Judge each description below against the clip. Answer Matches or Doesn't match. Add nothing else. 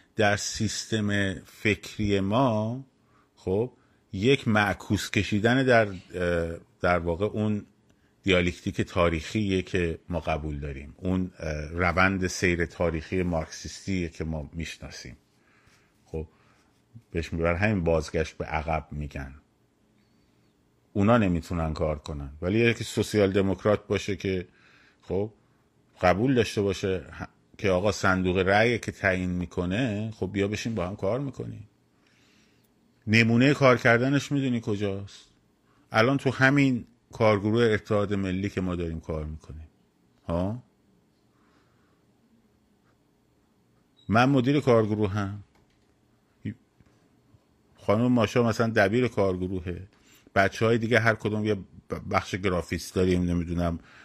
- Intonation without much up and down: Doesn't match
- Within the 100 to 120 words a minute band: Matches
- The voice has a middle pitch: Doesn't match